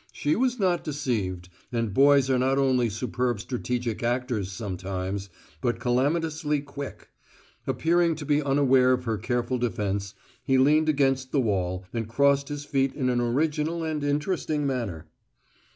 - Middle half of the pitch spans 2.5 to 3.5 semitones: No, average, 4.0 semitones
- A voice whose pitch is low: Yes, low, 130 Hz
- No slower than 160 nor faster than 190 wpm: No, average, 150 wpm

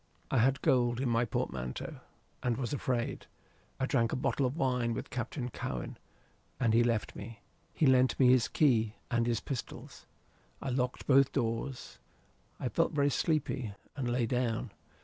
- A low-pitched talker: Yes, low, 125 Hz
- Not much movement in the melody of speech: Yes, narrow, 2.3 semitones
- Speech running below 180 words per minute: Yes, average, 165 wpm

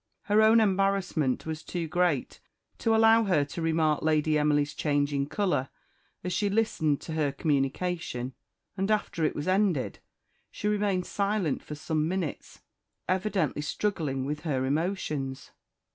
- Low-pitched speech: No, medium, 160 Hz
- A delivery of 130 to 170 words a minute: Yes, average, 140 wpm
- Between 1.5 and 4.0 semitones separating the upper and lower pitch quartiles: No, average, 5.1 semitones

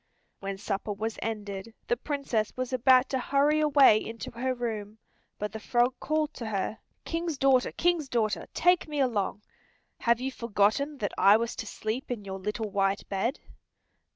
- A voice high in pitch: Yes, high, 235 Hz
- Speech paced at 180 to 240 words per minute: No, average, 170 wpm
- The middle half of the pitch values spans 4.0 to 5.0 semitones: Yes, average, 4.4 semitones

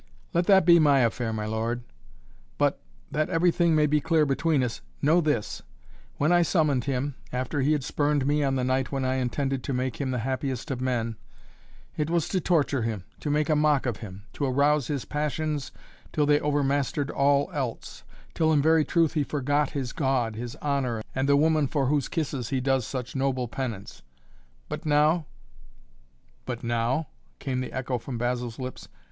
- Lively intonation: No, average, 3.2 semitones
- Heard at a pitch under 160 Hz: Yes, medium, 140 Hz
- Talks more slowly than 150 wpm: No, average, 190 wpm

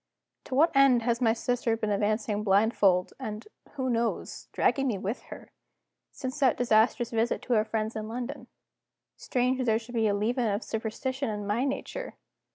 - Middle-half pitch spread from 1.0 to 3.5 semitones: Yes, average, 2.8 semitones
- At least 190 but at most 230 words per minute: No, average, 175 wpm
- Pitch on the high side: Yes, high, 230 Hz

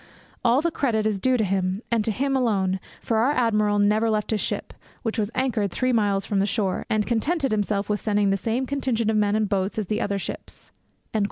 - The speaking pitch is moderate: No, high, 215 Hz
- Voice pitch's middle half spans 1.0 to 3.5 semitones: Yes, average, 2.8 semitones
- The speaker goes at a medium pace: No, fast, 225 wpm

